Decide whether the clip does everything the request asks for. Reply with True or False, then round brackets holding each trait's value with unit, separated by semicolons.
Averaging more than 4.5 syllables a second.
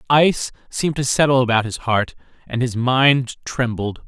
True (4.9 syllables/s)